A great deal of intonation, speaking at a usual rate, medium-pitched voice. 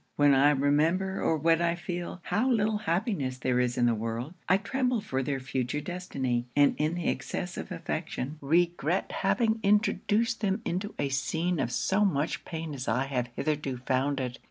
Yes: wide, 6.2 semitones; average, 180 wpm; medium, 155 Hz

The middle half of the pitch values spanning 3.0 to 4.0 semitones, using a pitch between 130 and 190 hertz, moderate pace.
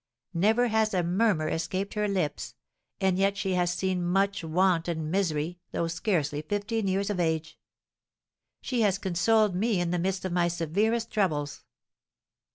Yes: average, 3.3 semitones; medium, 185 Hz; average, 160 wpm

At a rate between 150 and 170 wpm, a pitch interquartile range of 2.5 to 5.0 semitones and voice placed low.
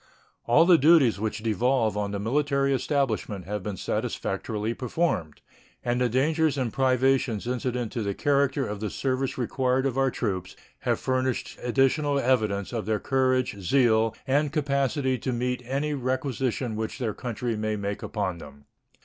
Yes: average, 160 wpm; average, 3.9 semitones; low, 125 Hz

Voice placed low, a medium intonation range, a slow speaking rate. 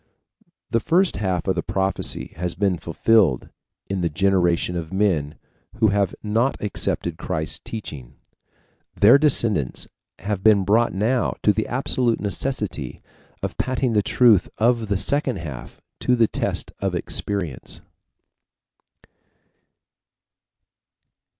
Yes: low, 100 Hz; average, 4.8 semitones; slow, 120 wpm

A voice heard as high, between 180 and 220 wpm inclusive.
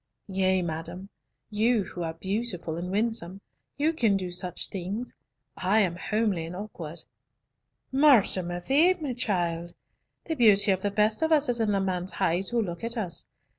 No: high, 195 Hz; average, 170 wpm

